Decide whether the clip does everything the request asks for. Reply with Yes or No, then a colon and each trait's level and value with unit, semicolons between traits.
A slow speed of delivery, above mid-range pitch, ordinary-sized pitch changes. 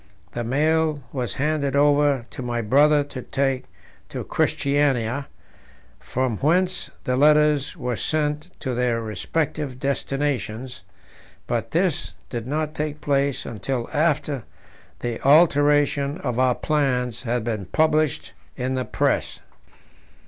No: slow, 120 wpm; medium, 140 Hz; average, 3.1 semitones